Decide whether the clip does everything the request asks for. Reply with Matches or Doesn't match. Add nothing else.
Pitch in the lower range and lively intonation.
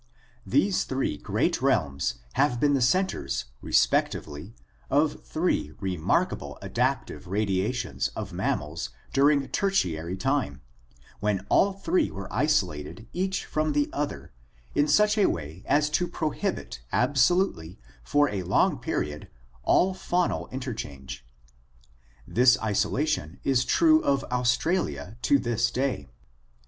Matches